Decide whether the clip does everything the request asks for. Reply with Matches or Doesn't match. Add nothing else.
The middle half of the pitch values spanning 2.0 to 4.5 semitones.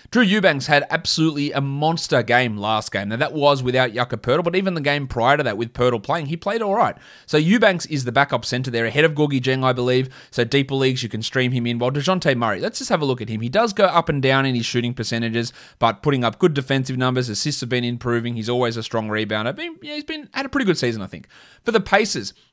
Doesn't match